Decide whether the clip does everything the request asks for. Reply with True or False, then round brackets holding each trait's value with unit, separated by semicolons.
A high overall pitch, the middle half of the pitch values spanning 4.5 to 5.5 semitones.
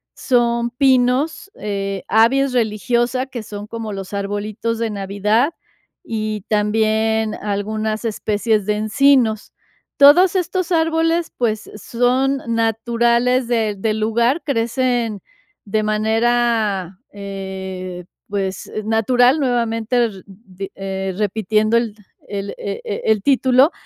False (220 Hz; 3.0 semitones)